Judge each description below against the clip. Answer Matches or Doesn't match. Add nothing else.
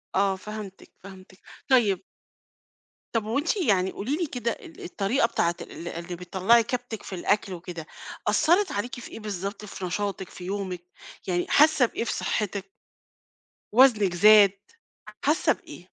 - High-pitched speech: Matches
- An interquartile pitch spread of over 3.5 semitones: Matches